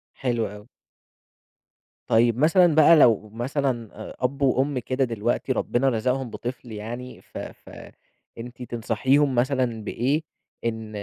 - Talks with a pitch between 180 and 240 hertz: No, low, 125 Hz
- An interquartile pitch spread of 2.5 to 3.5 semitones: Yes, average, 2.8 semitones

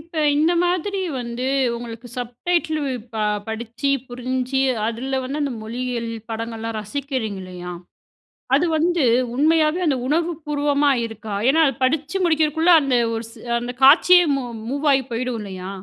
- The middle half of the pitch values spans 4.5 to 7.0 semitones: Yes, average, 4.9 semitones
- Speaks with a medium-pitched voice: No, very high, 265 Hz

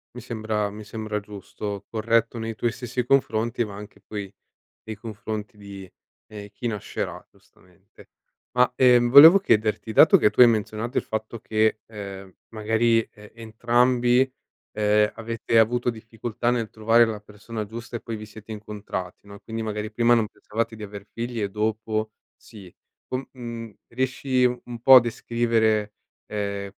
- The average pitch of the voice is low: Yes, low, 110 Hz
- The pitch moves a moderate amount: No, narrow, 2.0 semitones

